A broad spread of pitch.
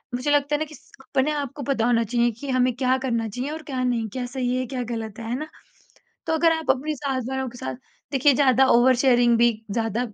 No: average, 2.8 semitones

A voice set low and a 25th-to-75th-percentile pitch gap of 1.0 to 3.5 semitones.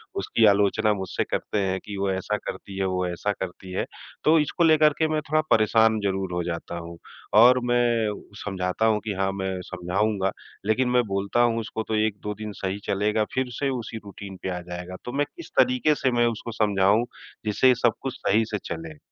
No: low, 105 Hz; average, 4.0 semitones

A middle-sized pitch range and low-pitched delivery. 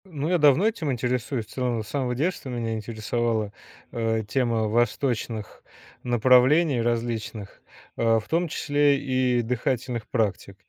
Yes: average, 3.4 semitones; low, 120 Hz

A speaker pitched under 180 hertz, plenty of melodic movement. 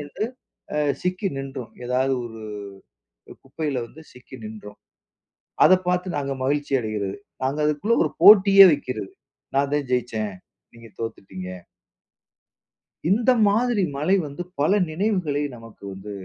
Yes: medium, 140 Hz; wide, 7.9 semitones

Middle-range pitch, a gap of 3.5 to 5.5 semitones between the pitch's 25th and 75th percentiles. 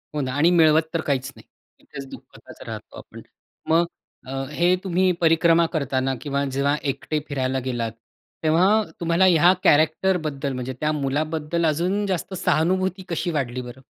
Yes: medium, 155 Hz; average, 3.9 semitones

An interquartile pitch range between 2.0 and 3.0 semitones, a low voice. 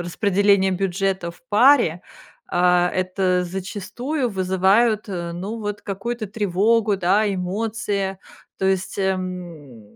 No: narrow, 2.4 semitones; high, 190 Hz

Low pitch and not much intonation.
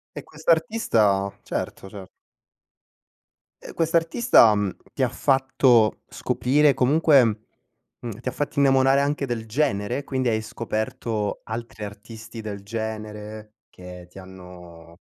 No: low, 110 Hz; average, 4.7 semitones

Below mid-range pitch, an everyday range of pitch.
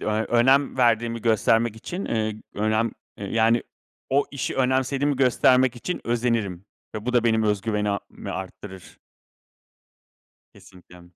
Yes: low, 115 Hz; average, 3.0 semitones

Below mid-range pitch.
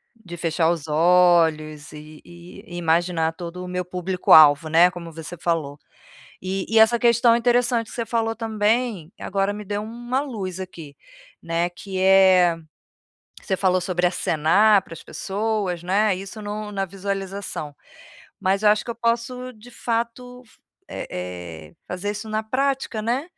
No: high, 190 Hz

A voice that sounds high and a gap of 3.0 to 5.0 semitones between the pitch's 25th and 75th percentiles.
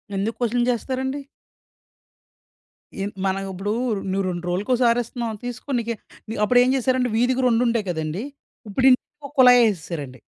Yes: high, 235 Hz; average, 4.4 semitones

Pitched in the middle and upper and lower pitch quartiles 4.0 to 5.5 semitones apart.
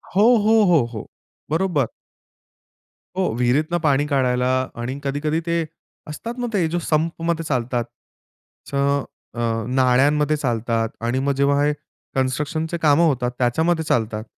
Yes: medium, 145 Hz; average, 4.4 semitones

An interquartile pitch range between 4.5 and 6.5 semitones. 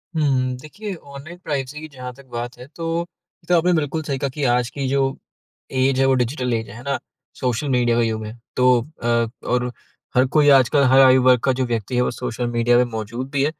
No: average, 2.7 semitones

